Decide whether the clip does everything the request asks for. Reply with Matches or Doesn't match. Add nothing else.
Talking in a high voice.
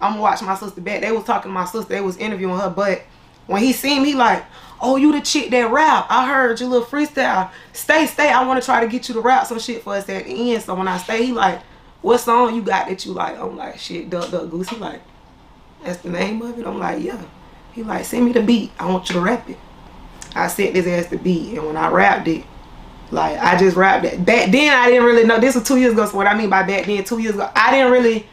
Matches